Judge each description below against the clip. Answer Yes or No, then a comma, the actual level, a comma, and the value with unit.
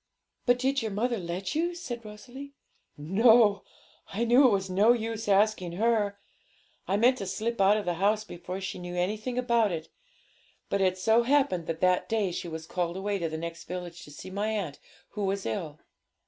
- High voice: Yes, high, 200 Hz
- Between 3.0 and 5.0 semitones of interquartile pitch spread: Yes, average, 4.3 semitones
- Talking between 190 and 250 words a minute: Yes, average, 195 wpm